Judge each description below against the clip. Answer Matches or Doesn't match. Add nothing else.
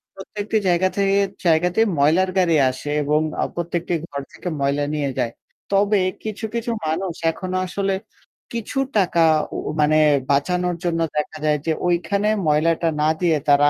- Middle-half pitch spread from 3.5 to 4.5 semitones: Matches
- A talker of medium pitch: Matches